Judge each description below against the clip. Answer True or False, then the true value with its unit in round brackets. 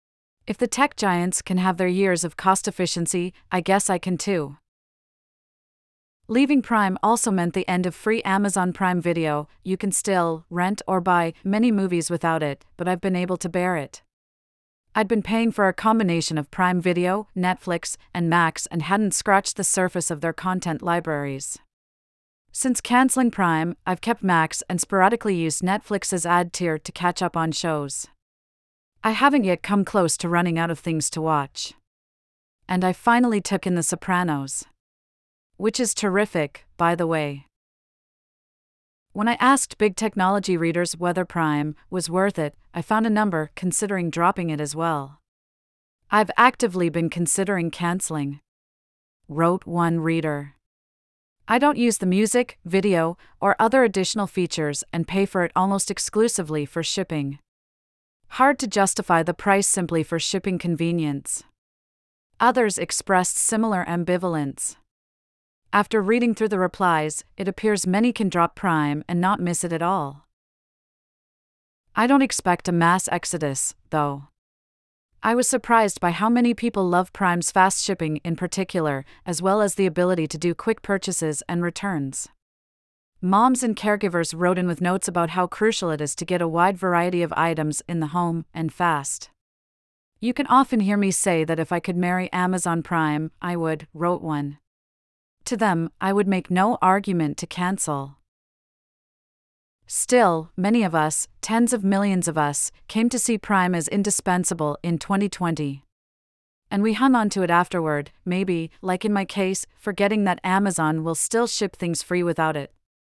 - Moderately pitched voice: True (180 Hz)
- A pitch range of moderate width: True (3.7 semitones)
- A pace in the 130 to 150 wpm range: False (160 wpm)